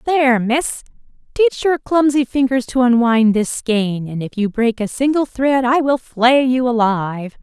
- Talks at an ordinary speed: Yes, average, 180 wpm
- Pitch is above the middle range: Yes, very high, 250 Hz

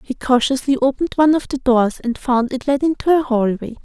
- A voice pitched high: Yes, very high, 260 Hz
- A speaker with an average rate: No, fast, 220 wpm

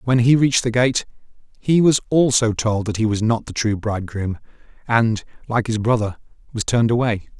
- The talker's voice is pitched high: No, low, 115 Hz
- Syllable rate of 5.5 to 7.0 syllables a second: Yes, 5.6 syllables/s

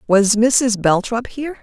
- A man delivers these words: No, female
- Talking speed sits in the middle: Yes, average, 145 wpm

